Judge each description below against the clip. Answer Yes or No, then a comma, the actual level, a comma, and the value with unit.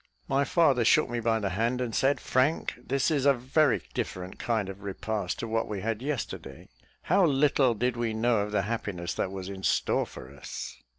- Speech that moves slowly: No, average, 200 wpm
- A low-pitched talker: Yes, low, 115 Hz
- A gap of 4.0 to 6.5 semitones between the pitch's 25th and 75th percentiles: Yes, average, 4.6 semitones